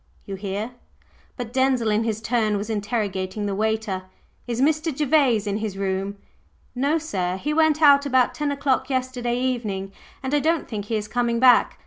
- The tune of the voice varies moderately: Yes, average, 4.4 semitones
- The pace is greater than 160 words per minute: Yes, average, 175 wpm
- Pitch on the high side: Yes, high, 235 Hz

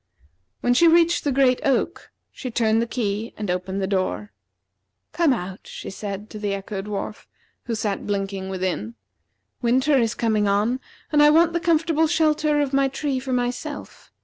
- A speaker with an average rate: Yes, average, 175 wpm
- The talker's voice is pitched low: No, high, 235 Hz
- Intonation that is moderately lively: No, wide, 6.4 semitones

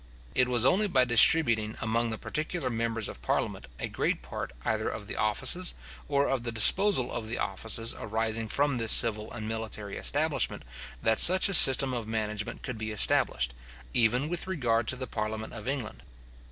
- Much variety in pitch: No, average, 3.6 semitones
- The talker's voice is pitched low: Yes, low, 115 Hz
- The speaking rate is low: No, average, 180 wpm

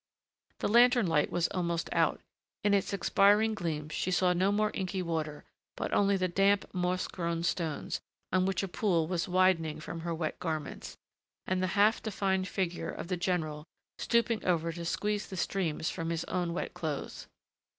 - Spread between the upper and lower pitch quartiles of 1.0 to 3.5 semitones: Yes, average, 2.9 semitones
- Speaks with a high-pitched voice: No, medium, 180 Hz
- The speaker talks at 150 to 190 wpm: Yes, average, 175 wpm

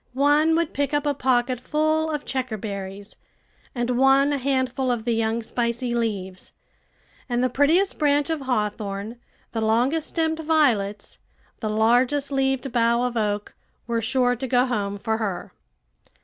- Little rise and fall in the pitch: No, average, 4.3 semitones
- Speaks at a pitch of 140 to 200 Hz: No, high, 245 Hz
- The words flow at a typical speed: Yes, average, 150 wpm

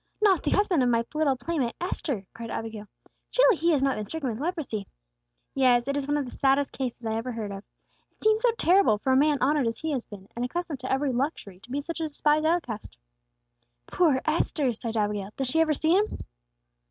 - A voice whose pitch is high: Yes, very high, 270 Hz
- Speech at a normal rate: No, fast, 220 wpm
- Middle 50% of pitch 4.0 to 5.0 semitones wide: No, wide, 5.5 semitones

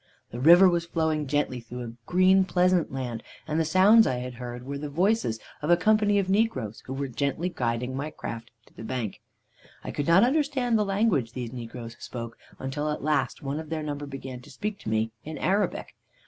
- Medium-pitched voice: Yes, medium, 145 Hz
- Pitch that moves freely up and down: Yes, wide, 6.8 semitones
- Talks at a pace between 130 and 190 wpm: No, fast, 205 wpm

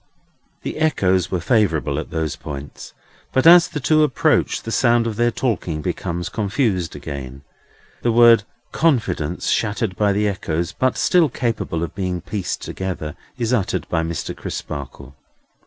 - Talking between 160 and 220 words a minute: No, average, 150 wpm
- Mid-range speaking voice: No, very low, 95 Hz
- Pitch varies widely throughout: Yes, wide, 6.5 semitones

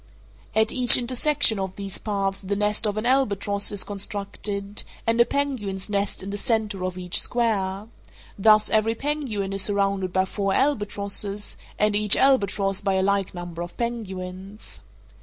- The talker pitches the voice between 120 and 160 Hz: No, high, 205 Hz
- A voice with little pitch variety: Yes, narrow, 2.1 semitones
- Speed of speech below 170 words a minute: Yes, average, 155 wpm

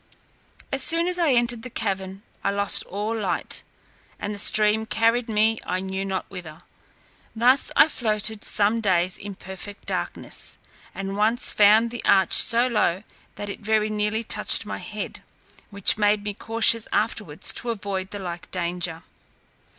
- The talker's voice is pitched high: Yes, high, 210 Hz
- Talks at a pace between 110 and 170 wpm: Yes, average, 160 wpm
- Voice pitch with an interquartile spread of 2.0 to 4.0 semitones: Yes, average, 2.8 semitones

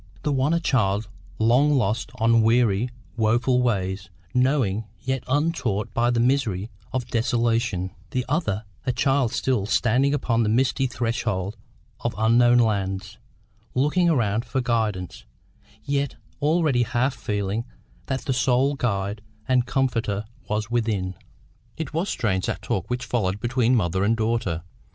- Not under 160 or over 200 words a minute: No, average, 140 wpm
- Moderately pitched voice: No, low, 120 Hz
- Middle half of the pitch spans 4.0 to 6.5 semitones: No, average, 3.6 semitones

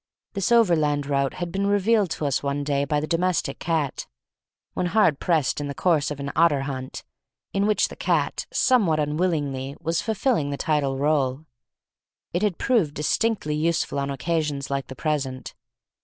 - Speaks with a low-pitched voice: No, medium, 150 Hz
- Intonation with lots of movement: No, average, 4.0 semitones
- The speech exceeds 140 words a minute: Yes, average, 170 wpm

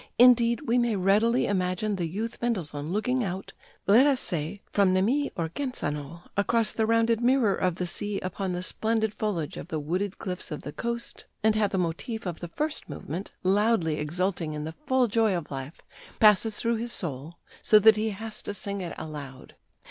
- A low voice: No, high, 200 Hz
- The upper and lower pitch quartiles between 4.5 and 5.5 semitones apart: Yes, average, 4.9 semitones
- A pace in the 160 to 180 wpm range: No, average, 190 wpm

